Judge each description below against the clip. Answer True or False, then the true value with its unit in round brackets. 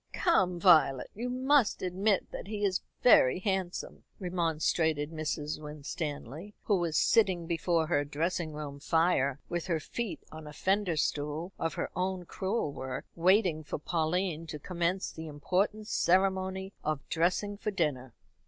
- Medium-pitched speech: True (175 Hz)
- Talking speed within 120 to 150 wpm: True (145 wpm)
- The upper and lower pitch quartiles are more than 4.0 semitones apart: False (3.7 semitones)